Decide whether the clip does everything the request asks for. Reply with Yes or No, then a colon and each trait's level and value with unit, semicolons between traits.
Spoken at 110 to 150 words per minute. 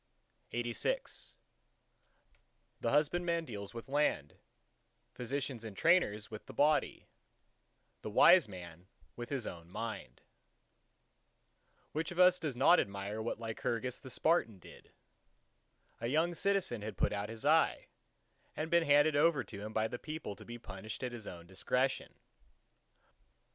Yes: average, 140 wpm